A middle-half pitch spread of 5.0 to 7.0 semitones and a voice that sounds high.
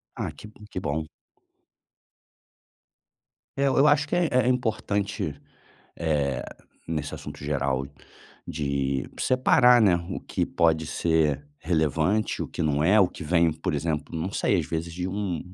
No: wide, 5.6 semitones; very low, 85 Hz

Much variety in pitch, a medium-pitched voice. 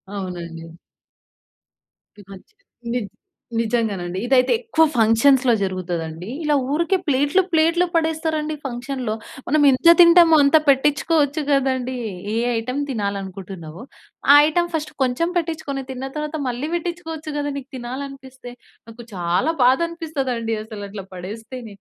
No: wide, 6.0 semitones; very high, 265 Hz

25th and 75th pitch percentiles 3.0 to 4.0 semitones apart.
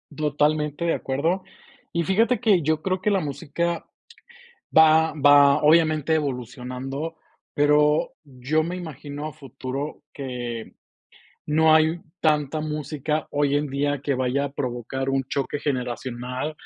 No: narrow, 2.6 semitones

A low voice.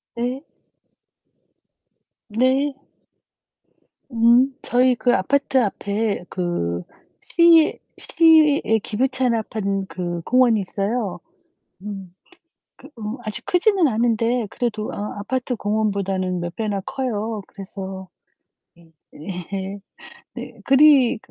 No: high, 220 Hz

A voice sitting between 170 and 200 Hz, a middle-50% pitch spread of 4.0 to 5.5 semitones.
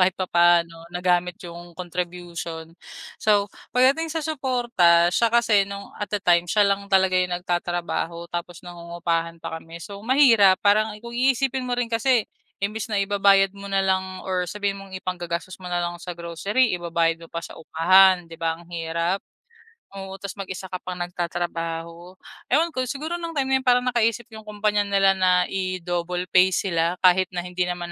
No: medium, 185 Hz; average, 3.2 semitones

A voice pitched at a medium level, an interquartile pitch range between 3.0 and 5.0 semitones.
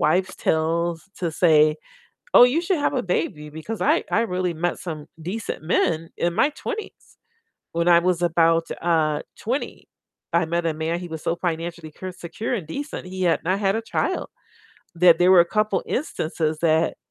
No: medium, 170 Hz; narrow, 2.6 semitones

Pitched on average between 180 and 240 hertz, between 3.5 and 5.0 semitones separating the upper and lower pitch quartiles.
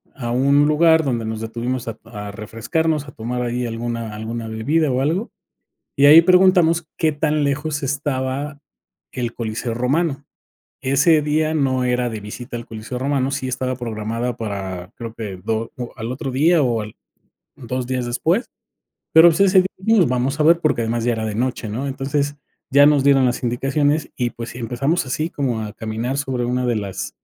No: low, 130 Hz; average, 4.1 semitones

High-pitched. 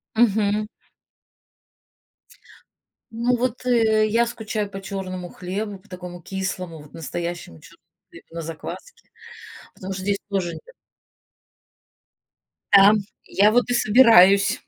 Yes: high, 200 Hz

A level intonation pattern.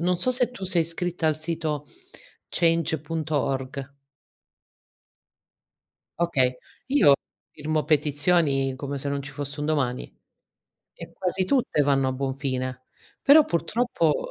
No: average, 3.7 semitones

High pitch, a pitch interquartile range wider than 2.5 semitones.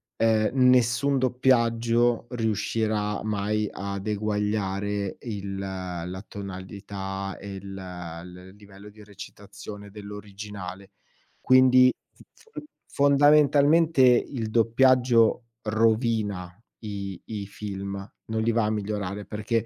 No: low, 105 Hz; average, 2.9 semitones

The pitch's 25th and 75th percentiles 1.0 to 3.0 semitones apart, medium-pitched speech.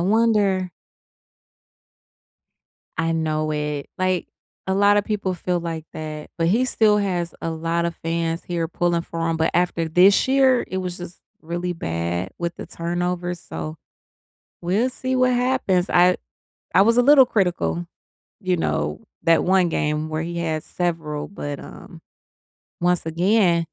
Yes: average, 2.7 semitones; medium, 175 Hz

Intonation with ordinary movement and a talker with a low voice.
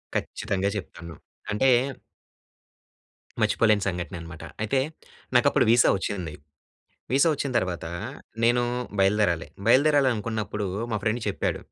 Yes: average, 4.4 semitones; low, 105 Hz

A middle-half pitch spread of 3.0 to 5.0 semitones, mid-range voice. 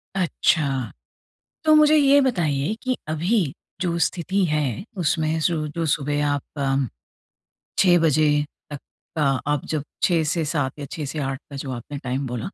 Yes: average, 3.6 semitones; medium, 155 Hz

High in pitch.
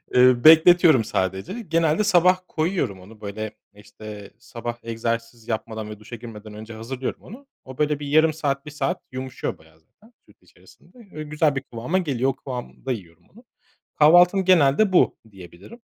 No: low, 130 Hz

